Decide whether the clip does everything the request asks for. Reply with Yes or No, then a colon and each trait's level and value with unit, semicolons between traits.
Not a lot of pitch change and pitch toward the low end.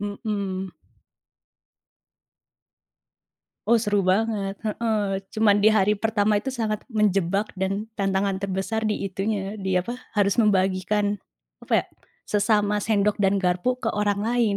No: narrow, 1.8 semitones; high, 205 Hz